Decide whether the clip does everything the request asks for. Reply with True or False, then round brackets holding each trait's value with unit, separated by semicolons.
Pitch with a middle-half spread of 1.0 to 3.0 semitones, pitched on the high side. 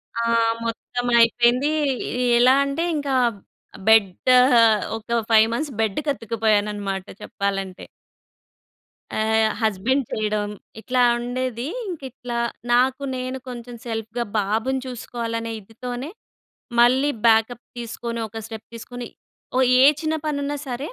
True (2.6 semitones; 235 Hz)